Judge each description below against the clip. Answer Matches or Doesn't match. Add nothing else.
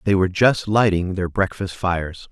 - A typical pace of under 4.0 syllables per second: Doesn't match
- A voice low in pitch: Matches